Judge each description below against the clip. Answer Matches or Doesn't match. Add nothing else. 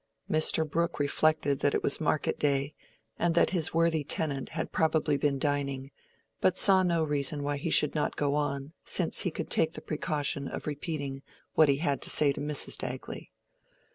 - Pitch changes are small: Matches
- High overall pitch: Doesn't match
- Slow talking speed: Doesn't match